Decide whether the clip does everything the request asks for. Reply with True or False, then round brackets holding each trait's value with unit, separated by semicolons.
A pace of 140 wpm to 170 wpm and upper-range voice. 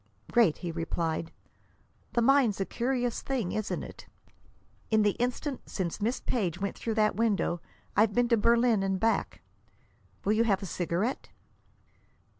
True (150 wpm; 215 Hz)